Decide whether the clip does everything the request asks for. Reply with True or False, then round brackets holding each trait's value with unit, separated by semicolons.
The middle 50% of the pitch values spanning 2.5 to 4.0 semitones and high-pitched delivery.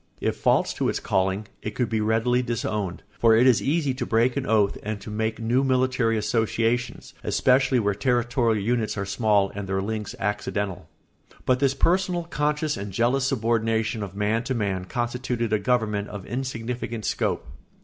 False (3.2 semitones; 115 Hz)